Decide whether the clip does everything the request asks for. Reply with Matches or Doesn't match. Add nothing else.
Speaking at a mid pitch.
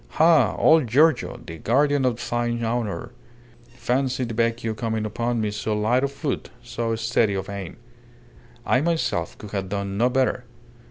Doesn't match